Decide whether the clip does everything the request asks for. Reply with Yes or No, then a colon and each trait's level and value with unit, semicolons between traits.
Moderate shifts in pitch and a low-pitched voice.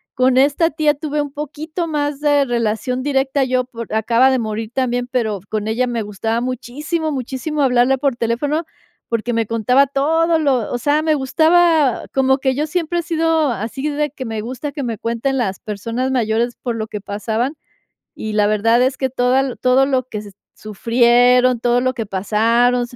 No: average, 3.7 semitones; very high, 255 Hz